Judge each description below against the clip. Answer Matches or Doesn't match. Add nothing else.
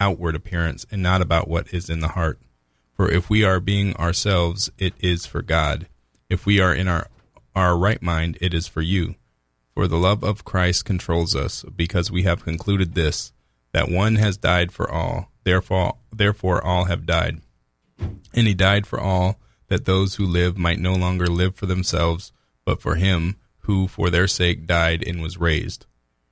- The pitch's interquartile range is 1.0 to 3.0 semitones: Matches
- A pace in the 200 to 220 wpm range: Doesn't match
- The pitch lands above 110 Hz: Doesn't match